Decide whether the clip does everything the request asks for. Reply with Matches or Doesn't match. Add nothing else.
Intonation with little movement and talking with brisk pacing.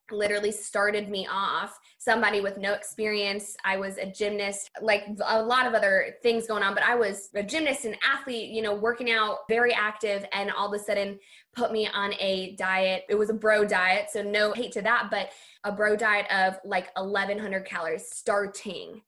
Doesn't match